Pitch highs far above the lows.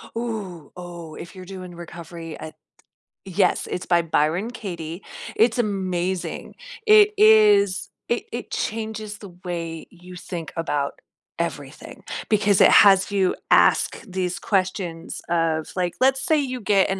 No: average, 4.0 semitones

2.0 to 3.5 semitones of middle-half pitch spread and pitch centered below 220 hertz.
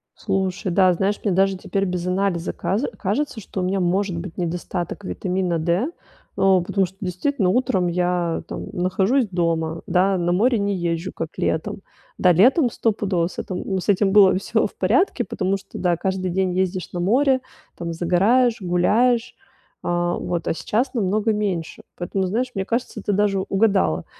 Yes: average, 2.7 semitones; high, 190 Hz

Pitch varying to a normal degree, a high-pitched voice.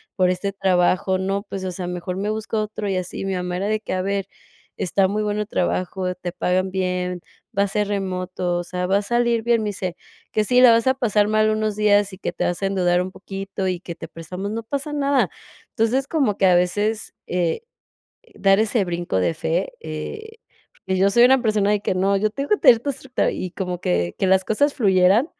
Yes: average, 3.0 semitones; high, 195 Hz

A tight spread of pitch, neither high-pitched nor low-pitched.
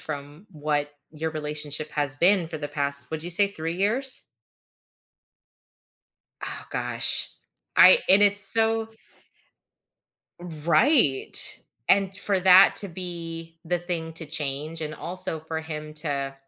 No: average, 3.8 semitones; medium, 165 Hz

